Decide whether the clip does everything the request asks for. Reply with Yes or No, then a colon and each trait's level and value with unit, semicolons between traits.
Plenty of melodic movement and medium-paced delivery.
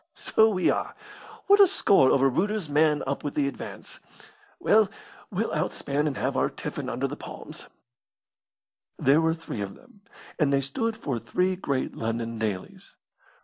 Yes: wide, 6.1 semitones; average, 160 wpm